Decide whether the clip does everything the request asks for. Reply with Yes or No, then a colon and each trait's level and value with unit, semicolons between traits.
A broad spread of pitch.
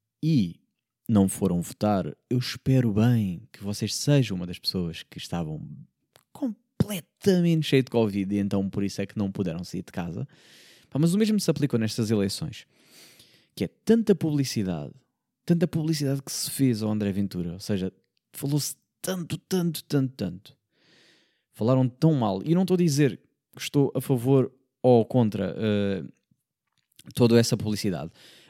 Yes: wide, 6.7 semitones